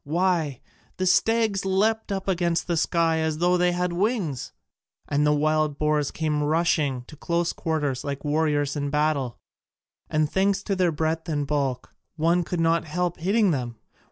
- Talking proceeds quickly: No, average, 165 wpm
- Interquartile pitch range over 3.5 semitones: No, average, 3.2 semitones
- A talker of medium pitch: Yes, medium, 160 Hz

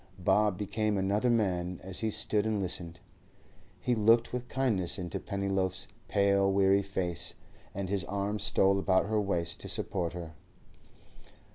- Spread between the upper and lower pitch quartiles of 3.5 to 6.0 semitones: No, narrow, 2.4 semitones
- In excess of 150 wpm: No, average, 145 wpm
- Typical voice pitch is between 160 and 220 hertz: No, low, 100 Hz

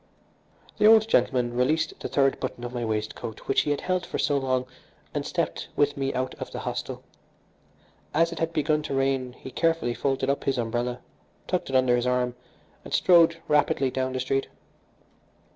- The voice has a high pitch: No, low, 135 Hz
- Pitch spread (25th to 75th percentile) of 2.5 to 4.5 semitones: Yes, average, 3.3 semitones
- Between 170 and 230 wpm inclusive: Yes, average, 185 wpm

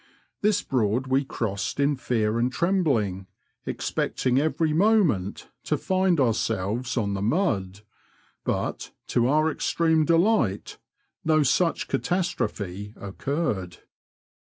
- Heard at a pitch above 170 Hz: No, low, 130 Hz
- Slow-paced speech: Yes, slow, 110 wpm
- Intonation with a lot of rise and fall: Yes, wide, 8.0 semitones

